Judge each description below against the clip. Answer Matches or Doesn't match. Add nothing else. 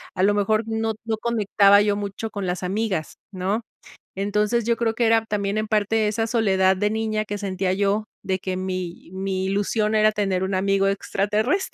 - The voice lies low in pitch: Doesn't match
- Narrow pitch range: Matches